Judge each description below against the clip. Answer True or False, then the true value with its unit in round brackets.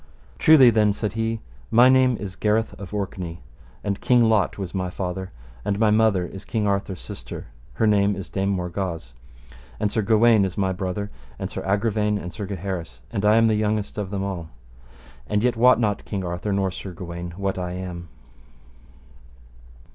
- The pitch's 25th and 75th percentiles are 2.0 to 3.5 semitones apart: True (2.6 semitones)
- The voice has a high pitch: False (100 Hz)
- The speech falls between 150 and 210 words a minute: True (180 wpm)